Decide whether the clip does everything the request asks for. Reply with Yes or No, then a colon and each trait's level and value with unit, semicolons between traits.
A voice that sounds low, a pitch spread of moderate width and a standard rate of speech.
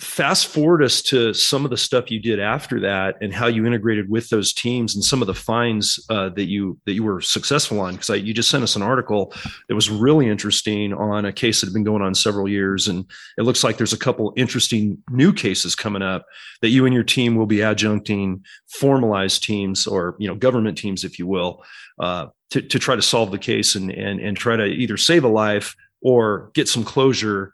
No: low, 110 Hz; average, 3.0 semitones; fast, 225 wpm